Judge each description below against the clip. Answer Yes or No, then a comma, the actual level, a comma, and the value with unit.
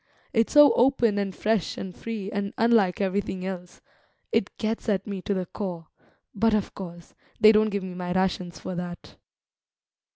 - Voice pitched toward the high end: Yes, high, 195 Hz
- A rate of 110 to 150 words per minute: No, average, 170 wpm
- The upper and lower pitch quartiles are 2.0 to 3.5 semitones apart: Yes, average, 3.0 semitones